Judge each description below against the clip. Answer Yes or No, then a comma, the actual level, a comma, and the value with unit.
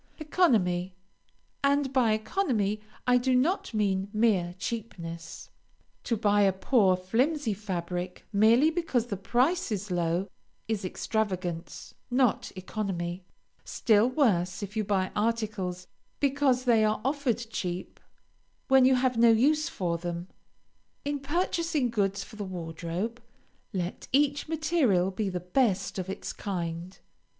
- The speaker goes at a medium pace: No, slow, 130 wpm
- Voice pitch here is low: No, high, 215 Hz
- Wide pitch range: Yes, wide, 5.7 semitones